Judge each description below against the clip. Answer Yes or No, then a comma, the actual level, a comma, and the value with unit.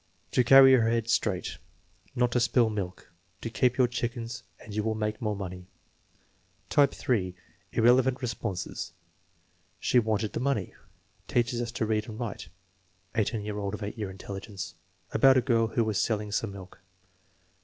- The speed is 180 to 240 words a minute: No, average, 165 wpm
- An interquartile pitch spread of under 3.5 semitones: Yes, average, 2.8 semitones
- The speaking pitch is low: Yes, low, 110 Hz